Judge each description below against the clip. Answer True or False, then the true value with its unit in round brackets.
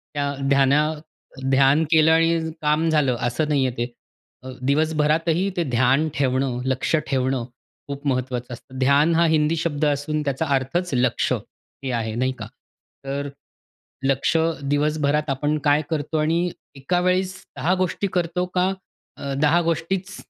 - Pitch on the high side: False (150 Hz)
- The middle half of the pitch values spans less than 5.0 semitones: True (3.3 semitones)